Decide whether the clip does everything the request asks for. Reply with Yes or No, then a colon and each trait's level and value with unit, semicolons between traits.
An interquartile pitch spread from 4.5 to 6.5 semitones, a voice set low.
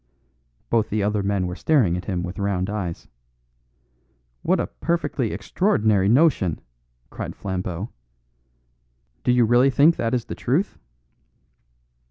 Yes: average, 5.0 semitones; low, 105 Hz